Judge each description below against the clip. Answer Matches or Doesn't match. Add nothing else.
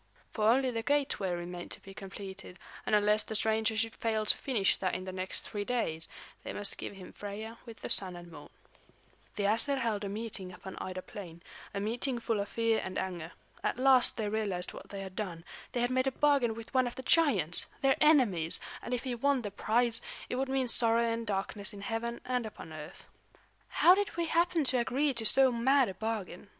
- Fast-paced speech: Matches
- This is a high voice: Matches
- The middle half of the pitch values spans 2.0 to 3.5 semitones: Doesn't match